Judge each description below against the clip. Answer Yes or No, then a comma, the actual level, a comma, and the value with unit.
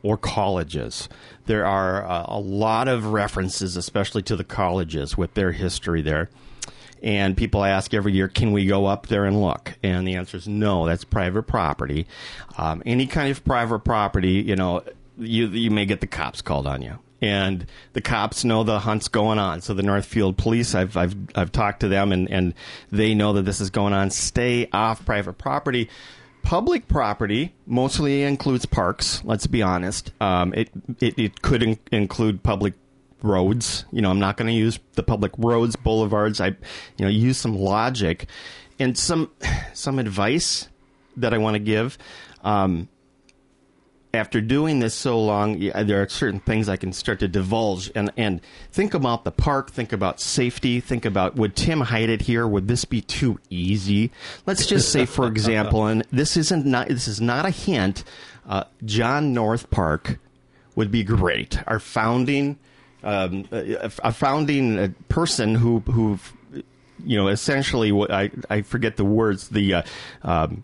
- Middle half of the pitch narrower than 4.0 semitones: Yes, average, 3.6 semitones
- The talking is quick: No, average, 175 wpm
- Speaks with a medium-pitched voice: No, low, 110 Hz